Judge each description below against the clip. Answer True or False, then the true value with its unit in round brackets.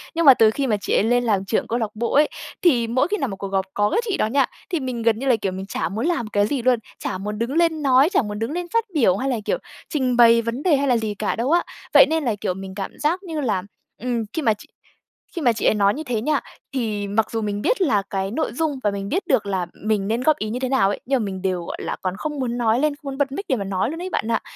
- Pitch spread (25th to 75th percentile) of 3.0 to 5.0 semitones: False (5.5 semitones)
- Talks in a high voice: True (235 Hz)